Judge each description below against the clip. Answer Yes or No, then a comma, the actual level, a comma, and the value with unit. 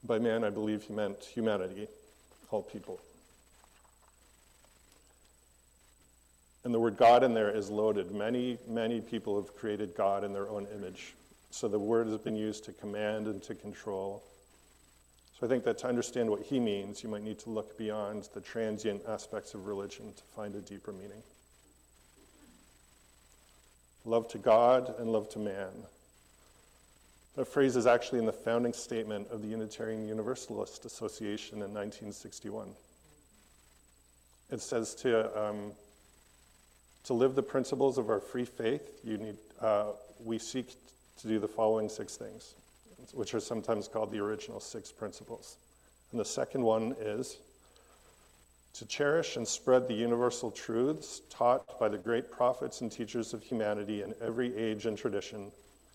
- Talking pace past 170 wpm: No, average, 150 wpm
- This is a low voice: Yes, low, 105 Hz